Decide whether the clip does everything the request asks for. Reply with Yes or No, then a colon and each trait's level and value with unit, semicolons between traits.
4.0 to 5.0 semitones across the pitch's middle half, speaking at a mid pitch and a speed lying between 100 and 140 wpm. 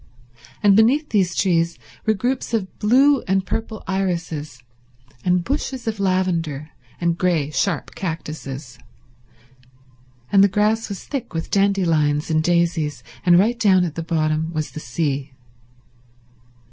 Yes: average, 4.5 semitones; medium, 180 Hz; slow, 135 wpm